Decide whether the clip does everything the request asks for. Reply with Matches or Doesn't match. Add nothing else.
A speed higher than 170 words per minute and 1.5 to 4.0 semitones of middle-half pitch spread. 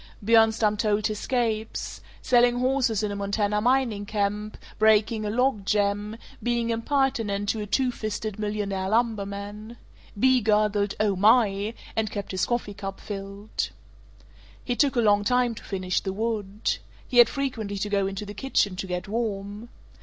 Doesn't match